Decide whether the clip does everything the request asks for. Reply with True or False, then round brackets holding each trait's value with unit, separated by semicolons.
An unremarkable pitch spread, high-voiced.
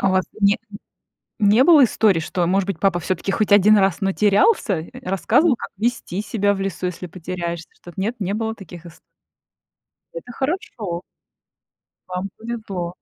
True (3.3 semitones; 195 Hz)